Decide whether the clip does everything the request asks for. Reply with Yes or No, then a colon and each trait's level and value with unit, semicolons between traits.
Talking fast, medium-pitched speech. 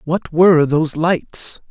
No: average, 140 wpm; medium, 160 Hz